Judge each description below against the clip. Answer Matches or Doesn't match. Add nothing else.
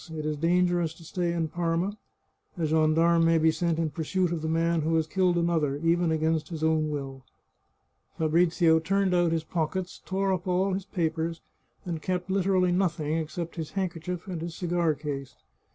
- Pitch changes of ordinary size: Doesn't match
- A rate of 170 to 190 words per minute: Matches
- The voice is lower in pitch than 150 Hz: Doesn't match